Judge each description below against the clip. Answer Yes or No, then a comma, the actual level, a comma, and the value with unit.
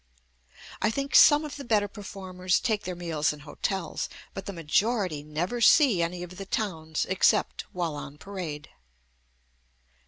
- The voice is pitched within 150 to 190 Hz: Yes, medium, 185 Hz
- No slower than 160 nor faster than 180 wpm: No, average, 150 wpm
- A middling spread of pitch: Yes, average, 4.5 semitones